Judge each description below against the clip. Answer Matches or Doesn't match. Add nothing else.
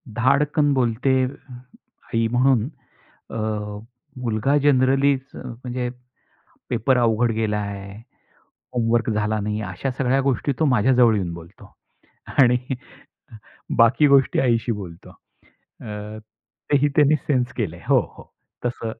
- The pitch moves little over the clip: Doesn't match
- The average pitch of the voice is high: Doesn't match